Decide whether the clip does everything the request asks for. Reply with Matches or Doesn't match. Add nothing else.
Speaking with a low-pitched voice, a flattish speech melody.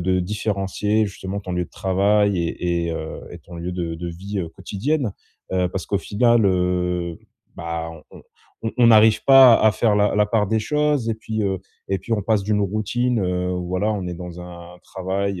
Doesn't match